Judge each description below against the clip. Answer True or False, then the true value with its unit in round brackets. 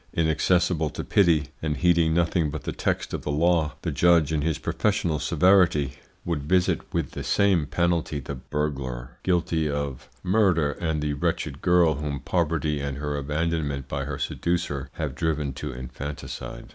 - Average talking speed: True (160 wpm)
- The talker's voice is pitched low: True (75 Hz)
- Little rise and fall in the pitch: False (3.0 semitones)